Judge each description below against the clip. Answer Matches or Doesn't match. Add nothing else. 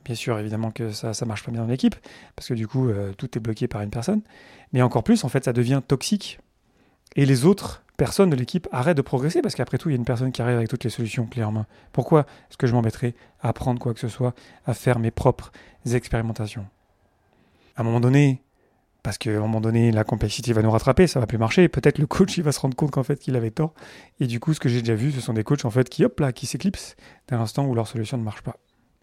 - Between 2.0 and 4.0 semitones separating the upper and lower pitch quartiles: Matches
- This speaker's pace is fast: Matches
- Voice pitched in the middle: Doesn't match